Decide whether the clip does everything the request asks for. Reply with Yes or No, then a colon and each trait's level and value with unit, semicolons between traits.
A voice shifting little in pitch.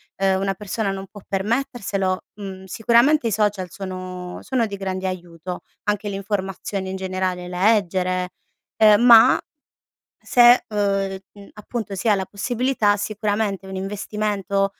Yes: narrow, 2.2 semitones